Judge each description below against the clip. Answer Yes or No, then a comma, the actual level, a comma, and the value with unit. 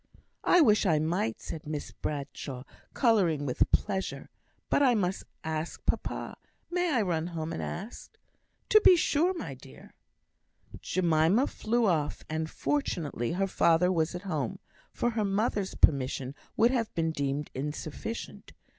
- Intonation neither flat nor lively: No, wide, 6.3 semitones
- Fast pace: No, average, 145 wpm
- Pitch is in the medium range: Yes, medium, 175 Hz